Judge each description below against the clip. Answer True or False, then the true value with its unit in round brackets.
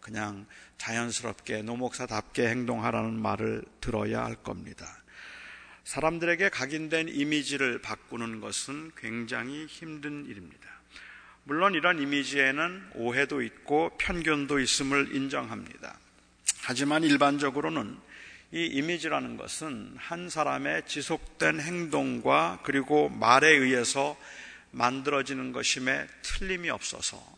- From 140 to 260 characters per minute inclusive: False (275 characters per minute)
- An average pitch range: True (4.3 semitones)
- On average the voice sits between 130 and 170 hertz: True (140 Hz)